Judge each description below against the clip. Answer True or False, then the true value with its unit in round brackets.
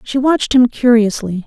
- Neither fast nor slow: True (165 wpm)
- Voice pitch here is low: False (240 Hz)